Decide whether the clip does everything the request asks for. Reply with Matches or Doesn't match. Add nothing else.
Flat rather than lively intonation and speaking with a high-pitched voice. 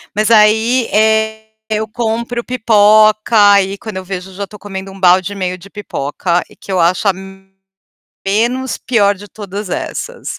Matches